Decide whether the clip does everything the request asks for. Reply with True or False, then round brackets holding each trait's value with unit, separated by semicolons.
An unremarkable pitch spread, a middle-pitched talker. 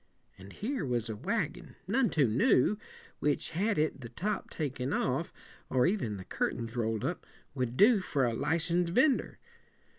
False (7.9 semitones; 145 Hz)